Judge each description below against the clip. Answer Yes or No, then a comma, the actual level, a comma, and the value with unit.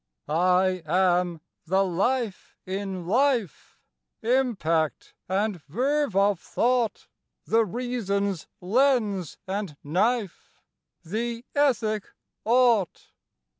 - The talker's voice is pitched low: No, high, 200 Hz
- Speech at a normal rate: No, slow, 85 wpm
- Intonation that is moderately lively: Yes, average, 4.7 semitones